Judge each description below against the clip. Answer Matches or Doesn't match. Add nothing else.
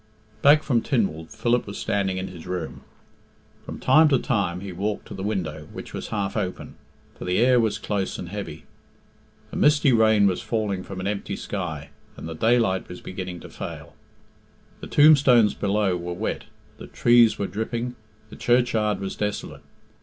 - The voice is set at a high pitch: Doesn't match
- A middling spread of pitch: Matches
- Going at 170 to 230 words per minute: Matches